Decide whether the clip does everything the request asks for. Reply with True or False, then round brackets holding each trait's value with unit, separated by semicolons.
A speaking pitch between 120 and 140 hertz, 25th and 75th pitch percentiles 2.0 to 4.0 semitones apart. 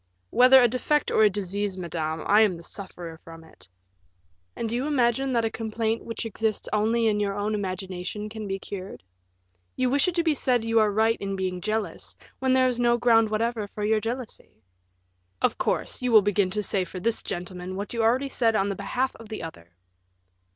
False (215 Hz; 3.3 semitones)